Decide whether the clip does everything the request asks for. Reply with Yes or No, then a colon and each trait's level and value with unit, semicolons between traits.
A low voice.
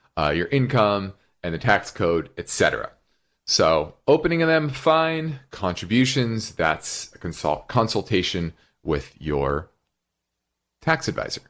Yes: low, 110 Hz